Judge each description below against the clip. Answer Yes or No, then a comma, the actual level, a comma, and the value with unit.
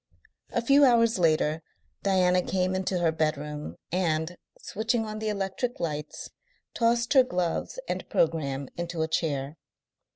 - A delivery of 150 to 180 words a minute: No, slow, 135 wpm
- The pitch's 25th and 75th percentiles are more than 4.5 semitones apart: Yes, wide, 5.5 semitones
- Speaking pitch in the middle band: Yes, medium, 180 Hz